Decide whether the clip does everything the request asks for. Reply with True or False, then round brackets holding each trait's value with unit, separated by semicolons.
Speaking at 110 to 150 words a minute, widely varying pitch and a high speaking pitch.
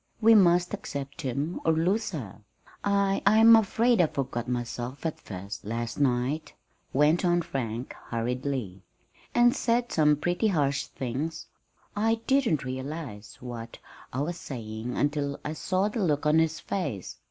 False (145 wpm; 6.8 semitones; 150 Hz)